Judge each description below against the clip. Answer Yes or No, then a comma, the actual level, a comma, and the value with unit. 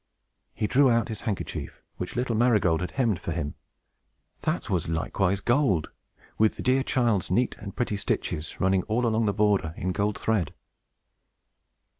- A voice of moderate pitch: No, low, 105 Hz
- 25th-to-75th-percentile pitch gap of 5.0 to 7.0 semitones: No, average, 4.3 semitones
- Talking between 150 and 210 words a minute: Yes, average, 160 wpm